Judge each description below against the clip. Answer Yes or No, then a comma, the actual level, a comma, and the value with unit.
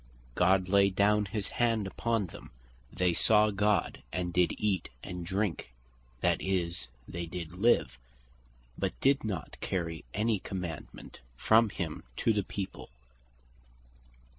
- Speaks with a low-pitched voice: Yes, very low, 95 Hz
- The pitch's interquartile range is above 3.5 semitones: No, average, 3.2 semitones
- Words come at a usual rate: No, slow, 125 wpm